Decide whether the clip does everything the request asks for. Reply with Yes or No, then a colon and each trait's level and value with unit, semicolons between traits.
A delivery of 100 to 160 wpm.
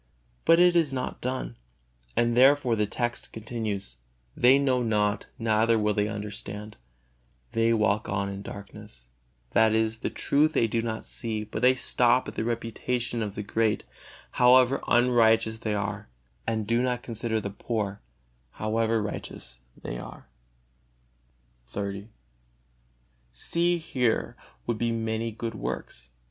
Yes: average, 140 wpm